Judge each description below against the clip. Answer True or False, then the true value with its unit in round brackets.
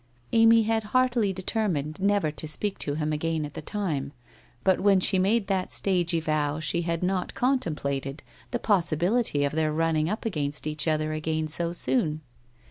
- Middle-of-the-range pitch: True (165 Hz)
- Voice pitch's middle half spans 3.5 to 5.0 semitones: True (4.7 semitones)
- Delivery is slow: False (170 wpm)